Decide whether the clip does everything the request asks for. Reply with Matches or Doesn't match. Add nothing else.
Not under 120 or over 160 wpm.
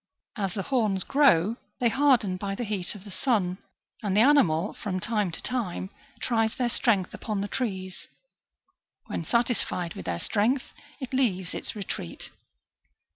Matches